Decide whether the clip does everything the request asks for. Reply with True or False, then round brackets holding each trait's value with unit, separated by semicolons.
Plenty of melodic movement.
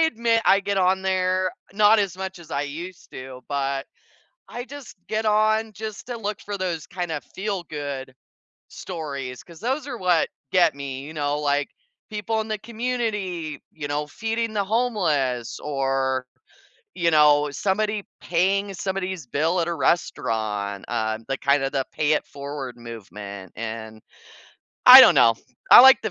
True (7.0 semitones)